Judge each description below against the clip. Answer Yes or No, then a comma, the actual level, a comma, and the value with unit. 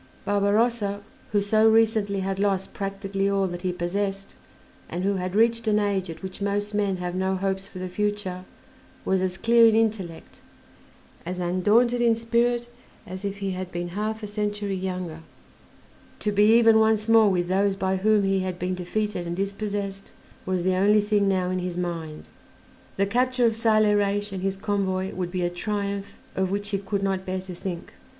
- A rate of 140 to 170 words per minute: No, average, 185 wpm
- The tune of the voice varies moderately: No, narrow, 2.1 semitones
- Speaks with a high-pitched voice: Yes, high, 195 Hz